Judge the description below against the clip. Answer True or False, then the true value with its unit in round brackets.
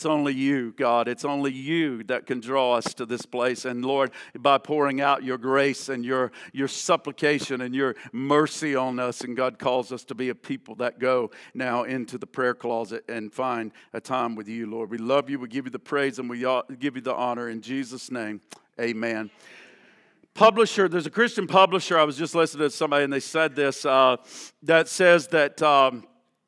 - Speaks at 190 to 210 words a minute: True (205 wpm)